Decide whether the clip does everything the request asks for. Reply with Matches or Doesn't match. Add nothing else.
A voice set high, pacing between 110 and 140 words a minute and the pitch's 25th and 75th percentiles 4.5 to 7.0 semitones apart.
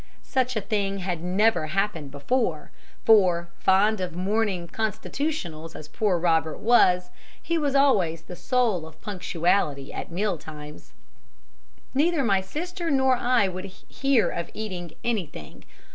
Matches